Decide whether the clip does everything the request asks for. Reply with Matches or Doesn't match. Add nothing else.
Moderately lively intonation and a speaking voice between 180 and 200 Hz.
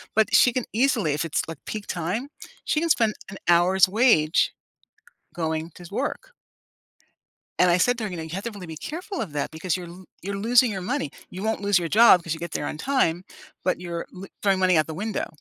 Matches